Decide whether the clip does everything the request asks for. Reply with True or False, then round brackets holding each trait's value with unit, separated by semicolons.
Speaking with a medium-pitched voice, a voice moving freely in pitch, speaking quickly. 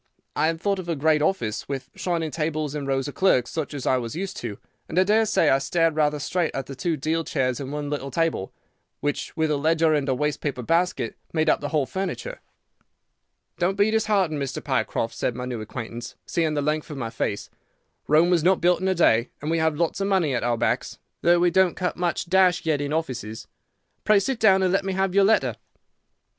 False (155 Hz; 4.6 semitones; 225 wpm)